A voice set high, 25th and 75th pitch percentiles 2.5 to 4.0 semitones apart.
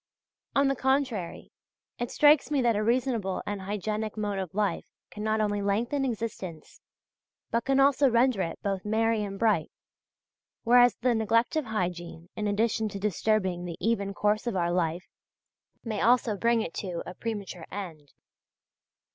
Yes: high, 215 Hz; average, 3.4 semitones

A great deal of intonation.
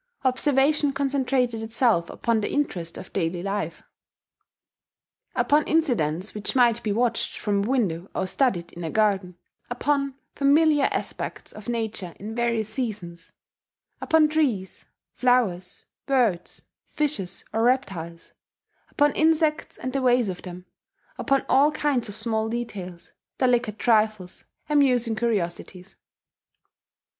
Yes: wide, 5.8 semitones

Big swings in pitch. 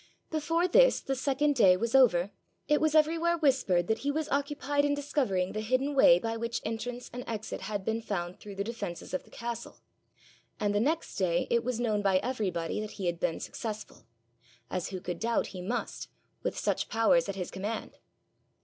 Yes: wide, 6.4 semitones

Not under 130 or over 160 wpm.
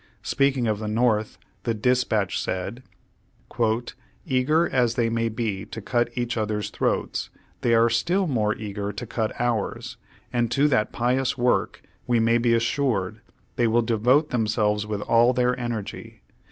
Yes: average, 155 wpm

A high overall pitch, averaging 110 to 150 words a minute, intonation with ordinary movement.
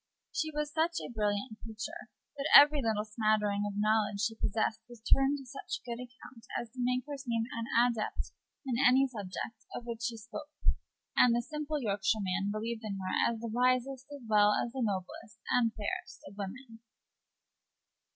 No: high, 230 Hz; average, 170 wpm; average, 3.5 semitones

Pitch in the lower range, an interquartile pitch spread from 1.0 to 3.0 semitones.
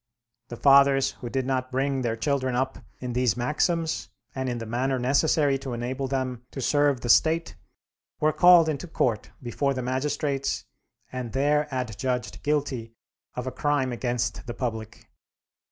Yes: low, 130 Hz; narrow, 2.5 semitones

